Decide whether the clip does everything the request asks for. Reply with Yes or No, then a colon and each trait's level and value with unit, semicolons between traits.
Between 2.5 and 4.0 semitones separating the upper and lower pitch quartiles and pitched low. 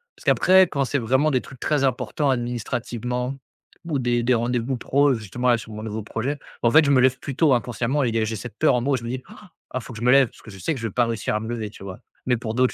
Yes: average, 2.9 semitones; low, 125 Hz